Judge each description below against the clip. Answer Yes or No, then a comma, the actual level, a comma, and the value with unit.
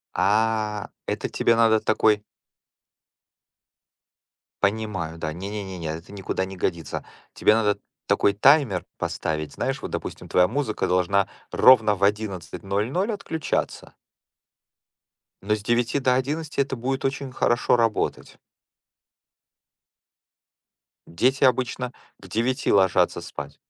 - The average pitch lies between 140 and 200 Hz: No, low, 105 Hz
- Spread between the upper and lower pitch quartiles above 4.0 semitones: Yes, average, 4.6 semitones